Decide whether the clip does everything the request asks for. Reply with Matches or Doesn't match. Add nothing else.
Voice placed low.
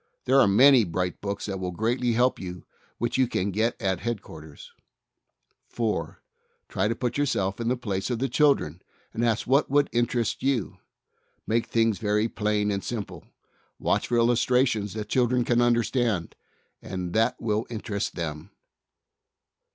Matches